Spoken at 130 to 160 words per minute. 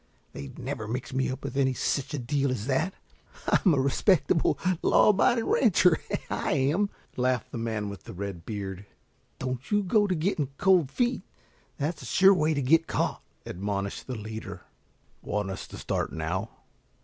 No: average, 170 wpm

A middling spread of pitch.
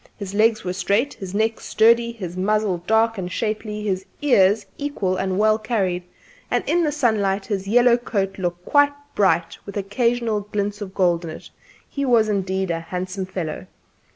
Yes: average, 3.2 semitones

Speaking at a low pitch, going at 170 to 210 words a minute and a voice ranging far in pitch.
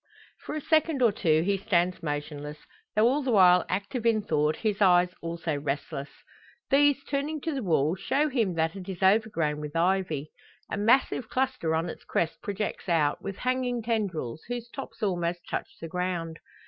No: high, 190 Hz; average, 175 wpm; wide, 6.3 semitones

